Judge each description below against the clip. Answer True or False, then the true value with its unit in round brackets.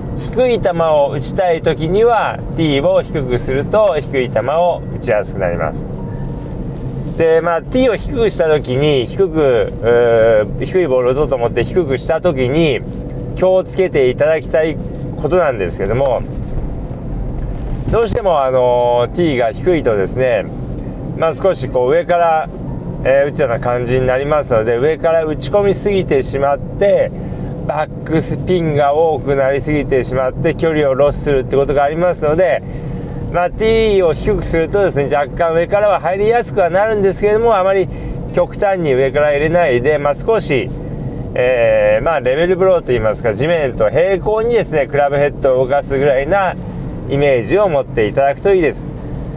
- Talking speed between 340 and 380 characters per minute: True (345 characters per minute)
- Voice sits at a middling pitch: True (155 Hz)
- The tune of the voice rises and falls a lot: False (4.8 semitones)